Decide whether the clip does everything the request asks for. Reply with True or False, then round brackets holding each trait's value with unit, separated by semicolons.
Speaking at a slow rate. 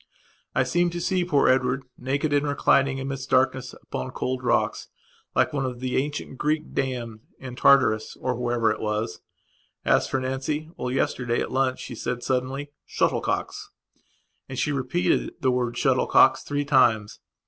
False (160 wpm)